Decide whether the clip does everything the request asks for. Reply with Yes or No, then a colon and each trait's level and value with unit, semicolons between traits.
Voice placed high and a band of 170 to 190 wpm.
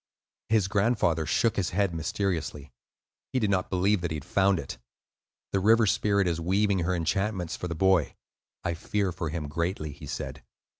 No: very low, 95 Hz; average, 180 wpm